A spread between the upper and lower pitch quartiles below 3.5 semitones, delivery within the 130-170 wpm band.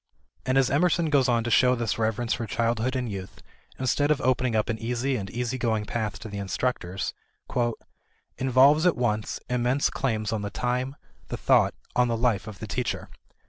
No: average, 2.9 semitones; average, 185 wpm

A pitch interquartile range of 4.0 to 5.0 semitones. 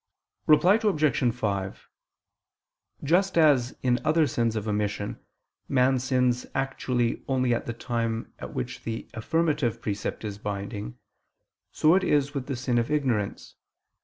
Yes: average, 4.6 semitones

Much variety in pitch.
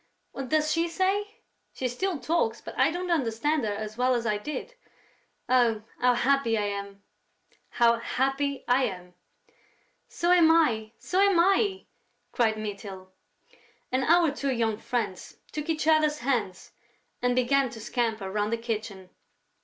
Yes: wide, 6.2 semitones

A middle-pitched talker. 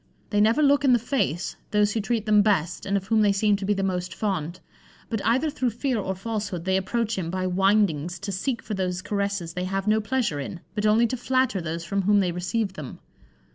No: high, 200 Hz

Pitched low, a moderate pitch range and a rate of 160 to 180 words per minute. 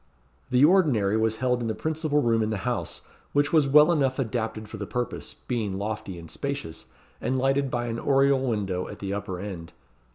No: low, 120 Hz; average, 4.7 semitones; average, 195 wpm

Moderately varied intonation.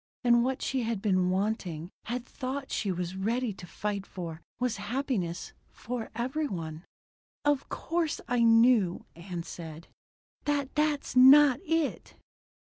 No: wide, 6.2 semitones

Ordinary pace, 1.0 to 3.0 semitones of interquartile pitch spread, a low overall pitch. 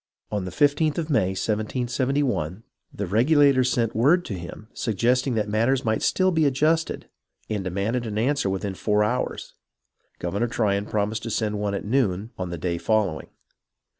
No: average, 165 wpm; average, 4.5 semitones; low, 110 Hz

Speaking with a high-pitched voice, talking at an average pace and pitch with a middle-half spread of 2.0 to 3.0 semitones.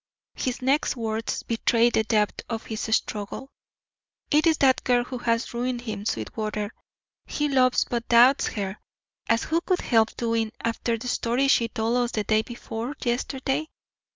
Yes: high, 235 Hz; average, 155 wpm; narrow, 2.5 semitones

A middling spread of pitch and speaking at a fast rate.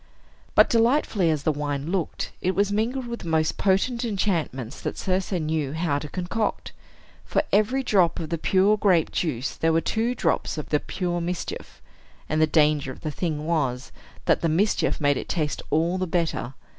No: average, 4.4 semitones; average, 185 wpm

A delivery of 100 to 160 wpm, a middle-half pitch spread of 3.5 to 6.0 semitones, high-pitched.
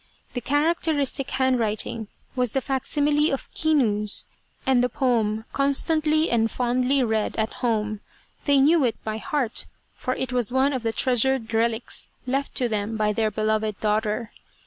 Yes: average, 150 wpm; average, 3.8 semitones; high, 245 Hz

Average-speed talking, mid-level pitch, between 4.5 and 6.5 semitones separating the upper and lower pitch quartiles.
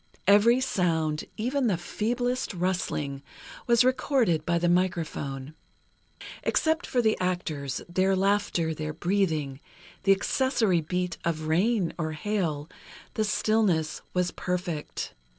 No: slow, 115 wpm; medium, 180 Hz; average, 5.2 semitones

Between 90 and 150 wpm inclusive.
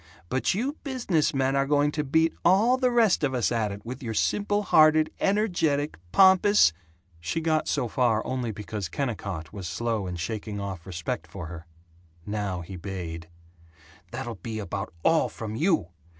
No: average, 170 wpm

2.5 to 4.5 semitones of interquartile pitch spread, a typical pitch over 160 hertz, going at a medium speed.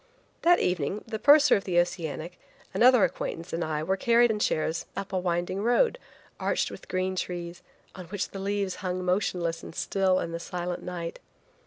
Yes: average, 2.9 semitones; medium, 185 Hz; average, 180 wpm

